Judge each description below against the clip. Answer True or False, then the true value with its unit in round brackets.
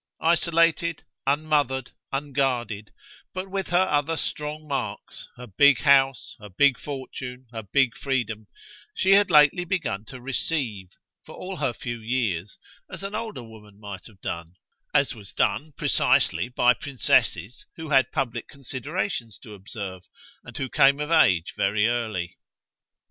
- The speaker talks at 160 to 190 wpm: False (145 wpm)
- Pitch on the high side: False (130 Hz)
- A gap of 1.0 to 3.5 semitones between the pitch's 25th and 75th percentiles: False (5.5 semitones)